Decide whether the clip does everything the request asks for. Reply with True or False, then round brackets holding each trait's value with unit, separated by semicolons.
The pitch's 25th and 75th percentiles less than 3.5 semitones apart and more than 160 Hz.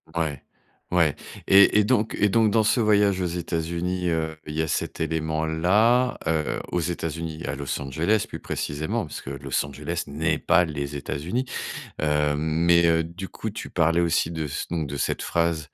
False (2.9 semitones; 80 Hz)